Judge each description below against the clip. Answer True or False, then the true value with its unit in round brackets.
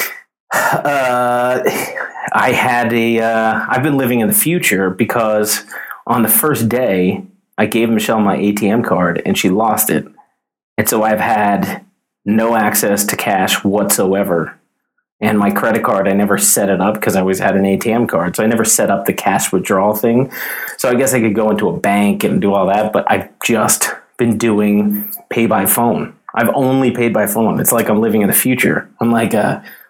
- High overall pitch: False (115 Hz)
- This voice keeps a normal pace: True (195 wpm)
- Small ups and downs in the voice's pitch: False (3.2 semitones)